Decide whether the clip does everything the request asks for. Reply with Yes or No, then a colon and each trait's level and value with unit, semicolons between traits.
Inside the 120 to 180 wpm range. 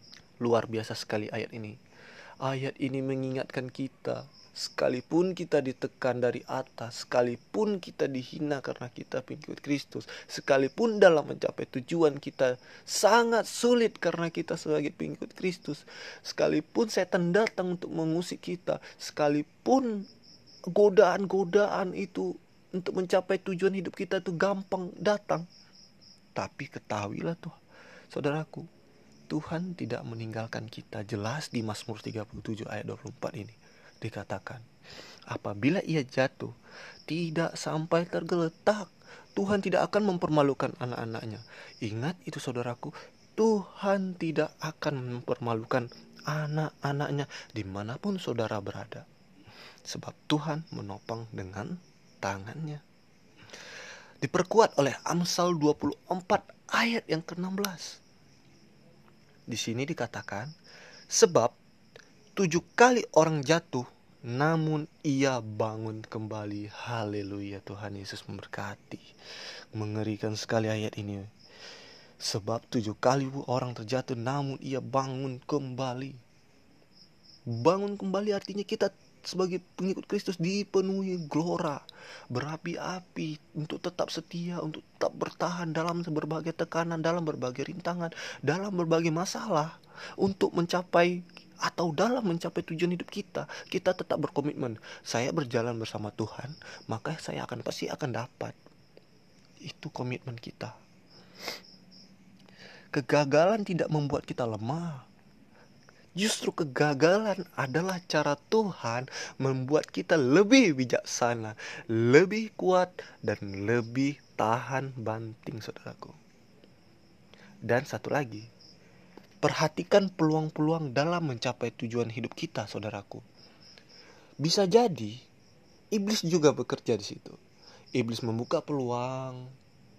No: average, 100 wpm